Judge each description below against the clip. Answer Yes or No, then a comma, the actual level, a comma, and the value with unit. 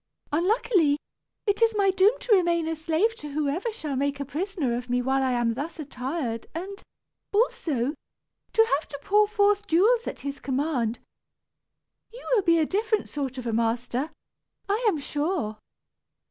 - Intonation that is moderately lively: No, wide, 7.1 semitones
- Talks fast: No, average, 165 wpm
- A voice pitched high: Yes, very high, 315 Hz